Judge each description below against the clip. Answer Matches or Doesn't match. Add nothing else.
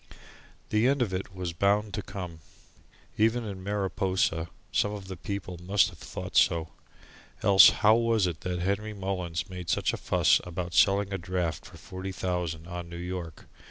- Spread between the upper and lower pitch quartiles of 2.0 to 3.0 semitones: Matches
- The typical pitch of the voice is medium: Doesn't match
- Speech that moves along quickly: Doesn't match